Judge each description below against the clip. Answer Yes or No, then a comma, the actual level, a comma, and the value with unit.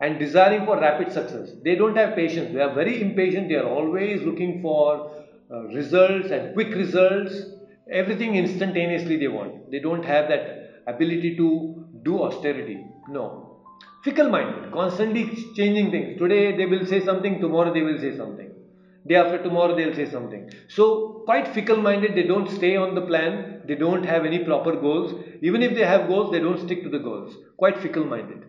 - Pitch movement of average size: Yes, average, 3.6 semitones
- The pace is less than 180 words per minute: No, average, 185 wpm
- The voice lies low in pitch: No, medium, 180 Hz